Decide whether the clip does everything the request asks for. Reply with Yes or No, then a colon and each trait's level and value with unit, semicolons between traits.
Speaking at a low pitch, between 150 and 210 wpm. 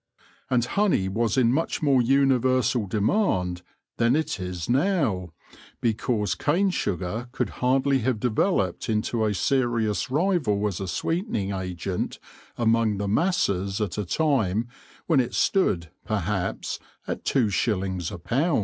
No: low, 115 Hz; average, 140 wpm